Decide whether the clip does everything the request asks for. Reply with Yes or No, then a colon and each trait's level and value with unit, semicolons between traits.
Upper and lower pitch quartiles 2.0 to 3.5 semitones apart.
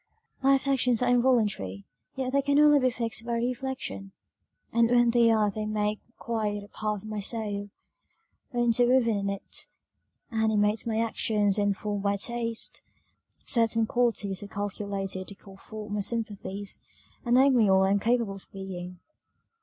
Yes: average, 2.9 semitones